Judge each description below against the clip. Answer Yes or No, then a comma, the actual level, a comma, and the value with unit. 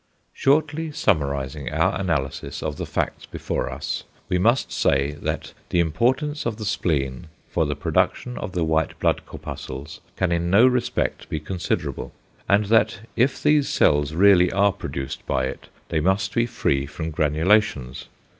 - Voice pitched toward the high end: No, very low, 90 Hz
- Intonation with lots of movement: Yes, wide, 7.3 semitones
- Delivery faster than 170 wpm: No, average, 155 wpm